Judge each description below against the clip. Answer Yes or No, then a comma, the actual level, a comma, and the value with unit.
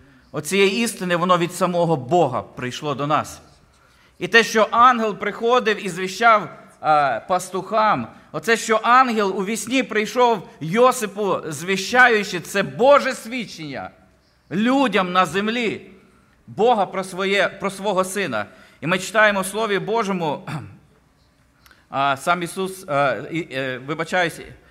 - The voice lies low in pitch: No, high, 195 Hz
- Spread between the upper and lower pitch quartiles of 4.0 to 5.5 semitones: Yes, average, 4.6 semitones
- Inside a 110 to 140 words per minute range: Yes, average, 125 wpm